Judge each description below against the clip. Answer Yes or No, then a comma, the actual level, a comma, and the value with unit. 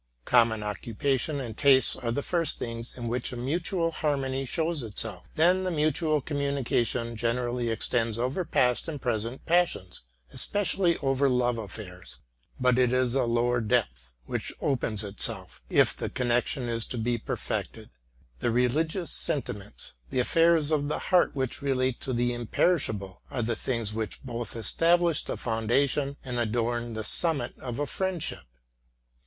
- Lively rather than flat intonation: No, average, 3.8 semitones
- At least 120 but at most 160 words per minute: Yes, average, 155 wpm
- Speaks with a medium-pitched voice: No, low, 125 Hz